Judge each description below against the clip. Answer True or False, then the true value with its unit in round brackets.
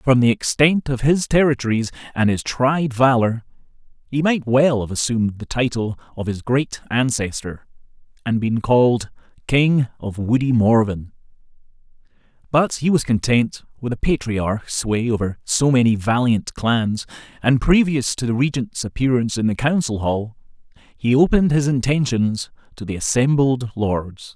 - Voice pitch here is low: True (125 Hz)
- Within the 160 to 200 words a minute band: False (145 wpm)